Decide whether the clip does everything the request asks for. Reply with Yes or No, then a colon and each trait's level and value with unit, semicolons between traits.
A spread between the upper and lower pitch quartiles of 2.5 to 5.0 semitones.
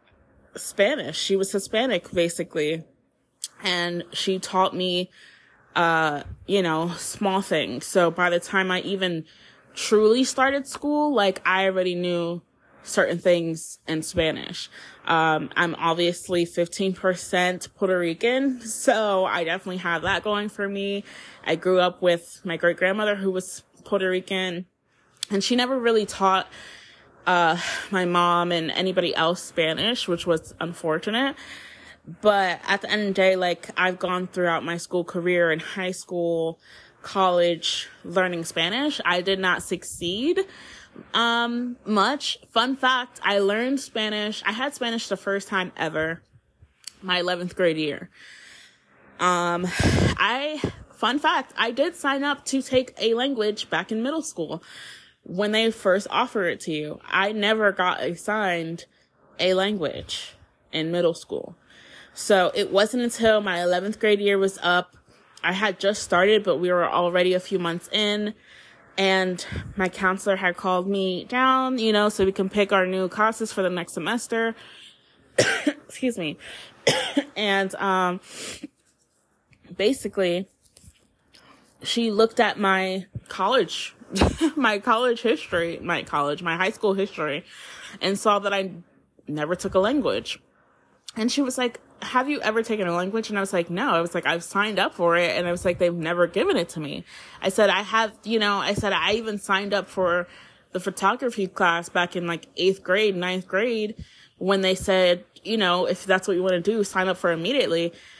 Yes: average, 3.4 semitones